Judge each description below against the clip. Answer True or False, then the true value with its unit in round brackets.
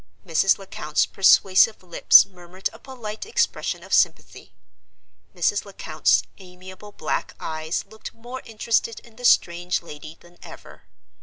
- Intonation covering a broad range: False (4.2 semitones)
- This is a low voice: False (185 Hz)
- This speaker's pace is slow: True (130 wpm)